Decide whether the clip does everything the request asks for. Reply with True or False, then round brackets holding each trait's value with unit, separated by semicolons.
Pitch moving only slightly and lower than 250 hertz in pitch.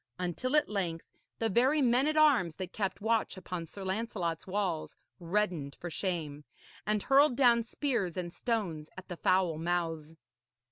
False (5.5 semitones; 190 Hz)